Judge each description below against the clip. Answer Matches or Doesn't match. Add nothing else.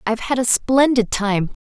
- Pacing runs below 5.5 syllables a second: Matches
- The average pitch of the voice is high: Matches